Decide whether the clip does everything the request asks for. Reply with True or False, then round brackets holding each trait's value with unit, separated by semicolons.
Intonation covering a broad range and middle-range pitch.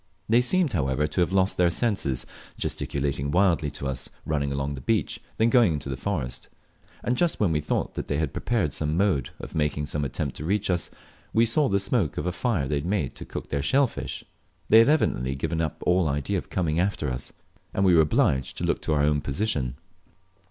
False (5.8 semitones; 80 Hz)